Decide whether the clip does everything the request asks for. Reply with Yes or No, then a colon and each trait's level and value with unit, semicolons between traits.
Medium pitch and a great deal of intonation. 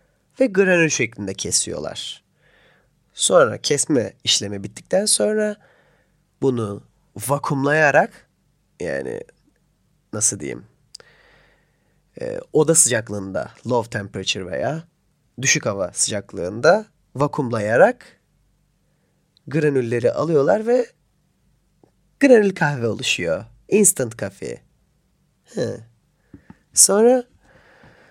Yes: medium, 145 Hz; wide, 8.2 semitones